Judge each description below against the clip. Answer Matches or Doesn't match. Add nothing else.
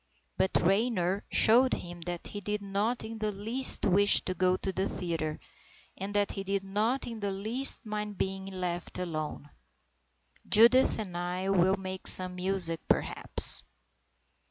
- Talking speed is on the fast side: Doesn't match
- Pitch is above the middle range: Matches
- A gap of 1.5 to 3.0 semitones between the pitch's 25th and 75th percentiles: Matches